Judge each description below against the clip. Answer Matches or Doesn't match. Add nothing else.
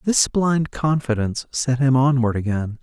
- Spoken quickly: Doesn't match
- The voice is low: Matches